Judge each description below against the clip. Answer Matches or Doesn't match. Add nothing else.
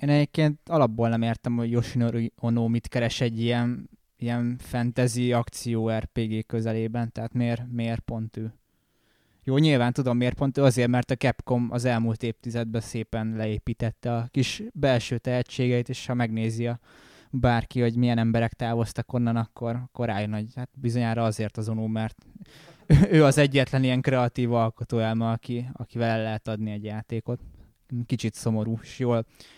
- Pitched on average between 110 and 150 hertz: Matches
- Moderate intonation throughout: Doesn't match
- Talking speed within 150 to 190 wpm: Matches